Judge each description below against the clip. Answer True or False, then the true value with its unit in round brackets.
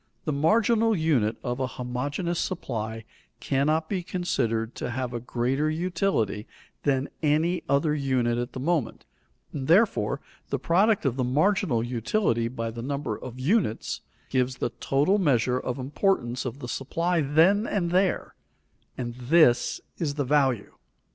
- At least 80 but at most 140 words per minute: False (150 wpm)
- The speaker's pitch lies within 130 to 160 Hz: True (140 Hz)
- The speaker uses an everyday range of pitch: False (5.8 semitones)